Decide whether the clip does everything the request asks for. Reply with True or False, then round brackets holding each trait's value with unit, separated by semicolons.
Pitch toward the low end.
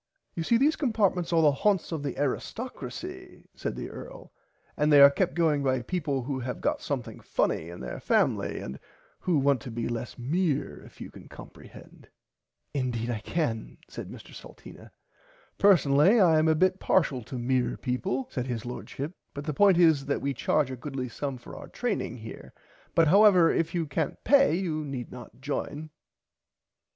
False (145 Hz)